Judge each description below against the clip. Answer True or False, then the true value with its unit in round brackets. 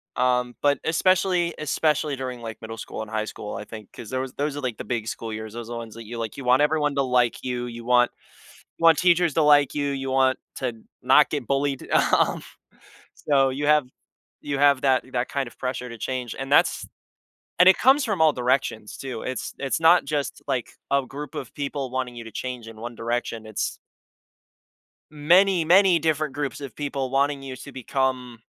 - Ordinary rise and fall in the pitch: True (3.3 semitones)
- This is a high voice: False (135 Hz)